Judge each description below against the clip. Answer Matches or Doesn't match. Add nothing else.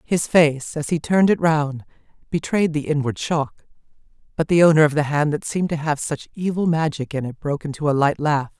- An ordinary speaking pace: Doesn't match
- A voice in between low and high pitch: Matches